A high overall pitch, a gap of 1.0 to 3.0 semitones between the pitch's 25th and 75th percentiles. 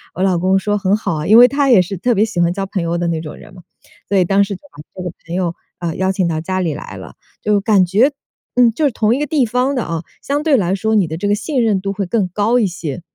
No: high, 195 Hz; average, 4.2 semitones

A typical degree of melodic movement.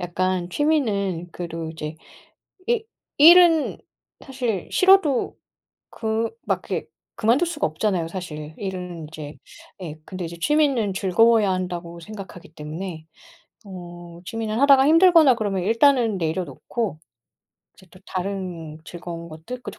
No: wide, 6.0 semitones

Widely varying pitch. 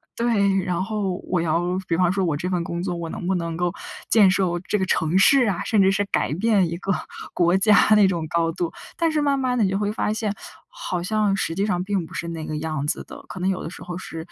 No: average, 3.4 semitones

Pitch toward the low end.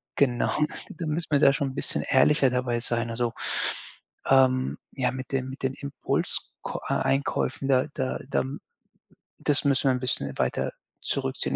Yes: low, 130 Hz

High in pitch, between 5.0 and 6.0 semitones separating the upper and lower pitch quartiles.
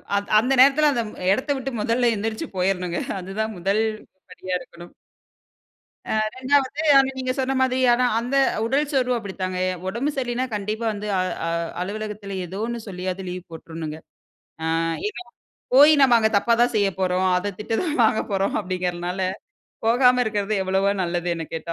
Yes: high, 210 Hz; average, 5.3 semitones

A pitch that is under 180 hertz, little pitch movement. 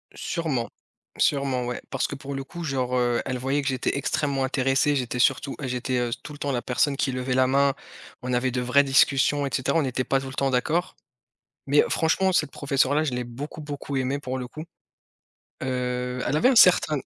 Yes: low, 135 Hz; narrow, 2.1 semitones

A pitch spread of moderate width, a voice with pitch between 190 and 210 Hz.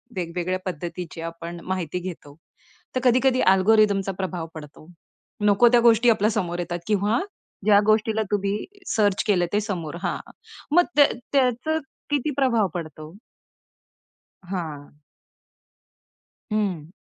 Yes: average, 4.2 semitones; high, 195 Hz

